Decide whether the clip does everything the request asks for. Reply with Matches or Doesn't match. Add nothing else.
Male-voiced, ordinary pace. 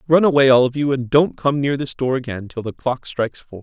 Doesn't match